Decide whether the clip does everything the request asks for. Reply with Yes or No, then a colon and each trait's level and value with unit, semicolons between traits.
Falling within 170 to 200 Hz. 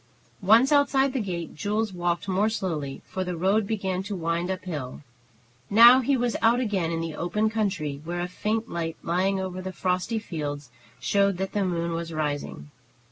Yes: medium, 185 Hz